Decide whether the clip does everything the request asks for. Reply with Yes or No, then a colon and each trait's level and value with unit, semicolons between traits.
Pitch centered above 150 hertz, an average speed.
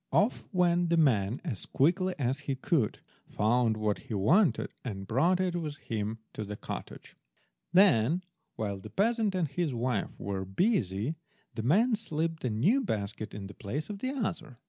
No: medium, 140 Hz; average, 170 wpm